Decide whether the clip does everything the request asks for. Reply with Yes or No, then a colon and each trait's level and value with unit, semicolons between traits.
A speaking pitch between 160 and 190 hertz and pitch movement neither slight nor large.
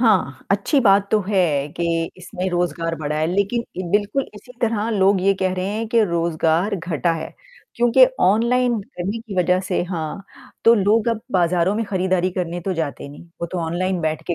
Yes: medium, 185 Hz; average, 3.6 semitones